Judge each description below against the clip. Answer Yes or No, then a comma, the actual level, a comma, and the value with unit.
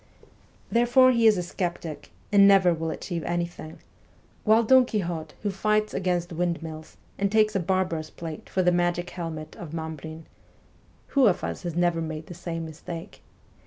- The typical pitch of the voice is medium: Yes, medium, 175 Hz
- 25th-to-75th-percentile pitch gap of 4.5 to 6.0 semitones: No, average, 3.4 semitones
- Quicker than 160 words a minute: Yes, average, 175 wpm